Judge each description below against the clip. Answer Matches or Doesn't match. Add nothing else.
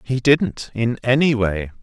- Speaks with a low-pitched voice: Matches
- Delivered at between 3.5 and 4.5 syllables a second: Matches